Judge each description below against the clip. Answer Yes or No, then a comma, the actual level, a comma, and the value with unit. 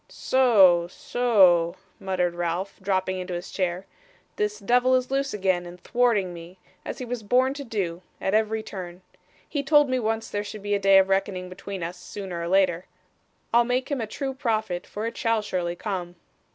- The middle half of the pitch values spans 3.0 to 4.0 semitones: No, average, 4.4 semitones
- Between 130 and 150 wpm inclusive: No, average, 190 wpm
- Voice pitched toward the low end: No, high, 200 Hz